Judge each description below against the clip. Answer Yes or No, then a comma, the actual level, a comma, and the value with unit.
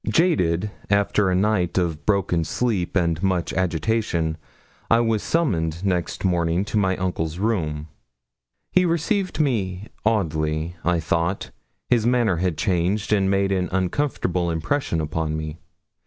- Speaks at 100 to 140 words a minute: Yes, slow, 135 wpm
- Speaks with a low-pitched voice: Yes, very low, 95 Hz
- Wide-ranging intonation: No, average, 4.3 semitones